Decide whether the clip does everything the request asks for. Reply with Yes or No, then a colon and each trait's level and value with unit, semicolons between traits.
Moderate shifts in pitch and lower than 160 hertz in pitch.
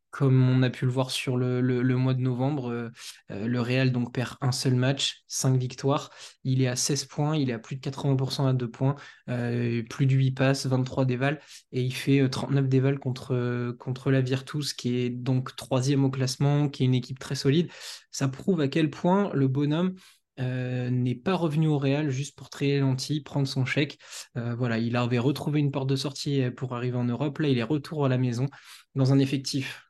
No: narrow, 1.9 semitones; low, 135 Hz